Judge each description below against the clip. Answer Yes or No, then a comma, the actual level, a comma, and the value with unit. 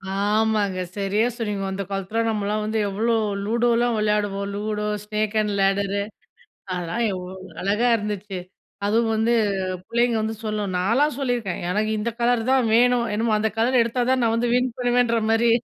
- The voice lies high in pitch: Yes, high, 220 Hz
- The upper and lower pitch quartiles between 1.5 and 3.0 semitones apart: Yes, narrow, 2.5 semitones